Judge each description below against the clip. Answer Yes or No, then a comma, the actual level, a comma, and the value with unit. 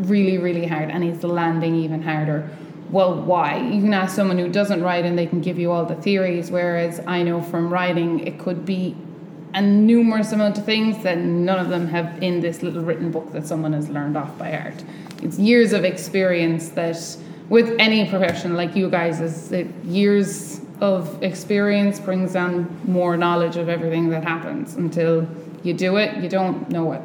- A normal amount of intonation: No, narrow, 2.2 semitones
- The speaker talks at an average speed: Yes, average, 195 wpm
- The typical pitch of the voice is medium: Yes, medium, 175 Hz